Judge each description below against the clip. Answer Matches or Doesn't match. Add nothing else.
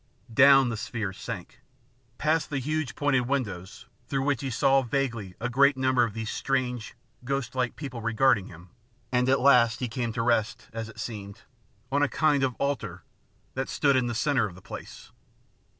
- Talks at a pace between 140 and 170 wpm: Doesn't match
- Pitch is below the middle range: Matches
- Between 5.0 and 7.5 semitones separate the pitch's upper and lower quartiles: Doesn't match